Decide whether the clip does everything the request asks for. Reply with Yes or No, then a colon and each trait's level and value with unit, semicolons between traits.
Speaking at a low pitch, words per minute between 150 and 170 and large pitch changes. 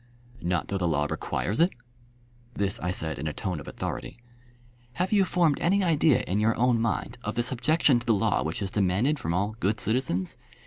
No: low, 110 Hz; fast, 205 wpm; wide, 6.5 semitones